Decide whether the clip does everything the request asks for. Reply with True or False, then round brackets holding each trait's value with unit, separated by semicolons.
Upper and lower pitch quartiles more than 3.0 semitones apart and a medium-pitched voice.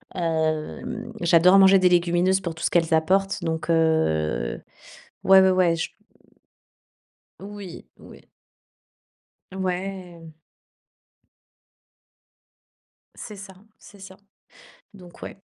False (2.7 semitones; 180 Hz)